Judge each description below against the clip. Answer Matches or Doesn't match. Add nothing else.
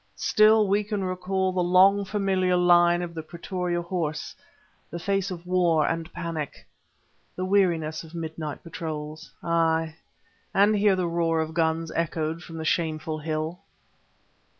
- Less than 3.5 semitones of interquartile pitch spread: Matches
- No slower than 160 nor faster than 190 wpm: Doesn't match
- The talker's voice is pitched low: Doesn't match